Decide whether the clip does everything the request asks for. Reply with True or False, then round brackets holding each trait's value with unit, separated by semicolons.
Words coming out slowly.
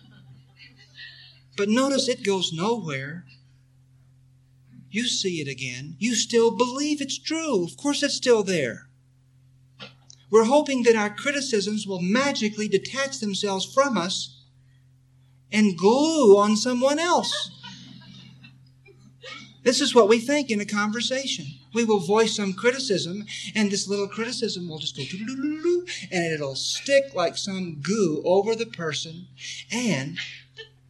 True (125 wpm)